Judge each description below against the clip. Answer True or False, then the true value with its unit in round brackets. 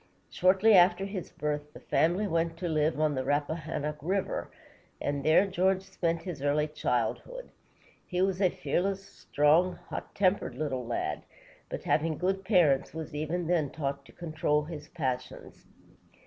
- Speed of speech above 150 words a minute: True (160 wpm)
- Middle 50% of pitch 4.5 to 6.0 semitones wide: False (3.7 semitones)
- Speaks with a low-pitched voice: False (165 Hz)